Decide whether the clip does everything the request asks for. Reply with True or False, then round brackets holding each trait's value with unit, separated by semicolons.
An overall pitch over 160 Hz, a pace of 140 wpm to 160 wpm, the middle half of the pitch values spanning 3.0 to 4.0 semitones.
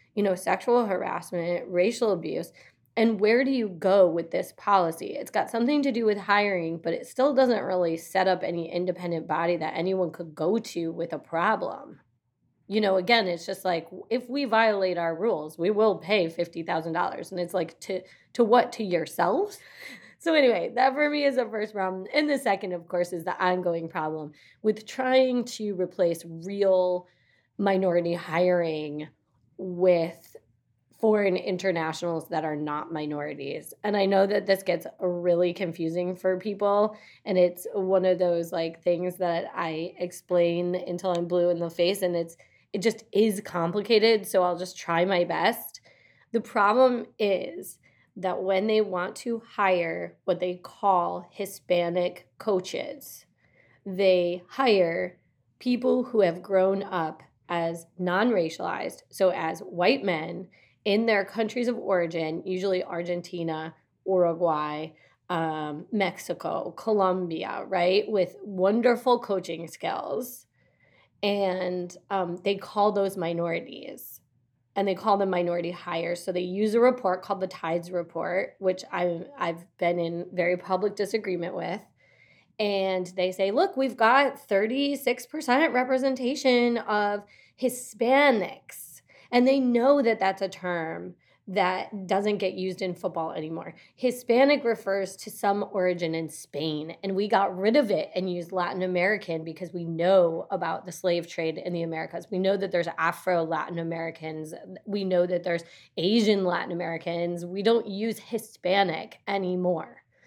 True (185 Hz; 150 wpm; 3.3 semitones)